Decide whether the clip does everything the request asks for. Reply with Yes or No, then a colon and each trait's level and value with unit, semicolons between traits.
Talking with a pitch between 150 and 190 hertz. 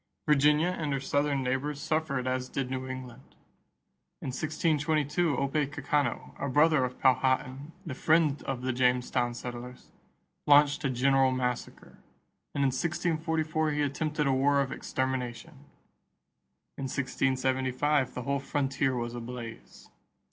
No: low, 135 Hz